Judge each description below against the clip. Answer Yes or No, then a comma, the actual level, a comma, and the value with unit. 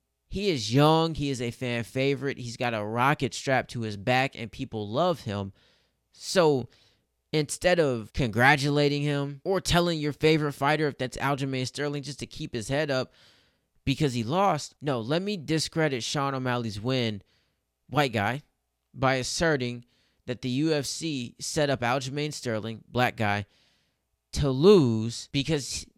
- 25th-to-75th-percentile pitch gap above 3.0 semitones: Yes, average, 4.0 semitones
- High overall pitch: No, low, 135 Hz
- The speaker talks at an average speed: Yes, average, 150 wpm